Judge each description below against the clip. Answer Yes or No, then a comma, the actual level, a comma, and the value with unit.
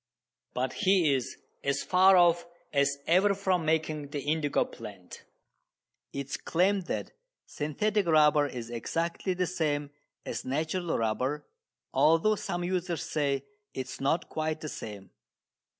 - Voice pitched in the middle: Yes, medium, 155 Hz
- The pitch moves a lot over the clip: No, average, 4.1 semitones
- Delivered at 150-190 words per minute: No, slow, 135 wpm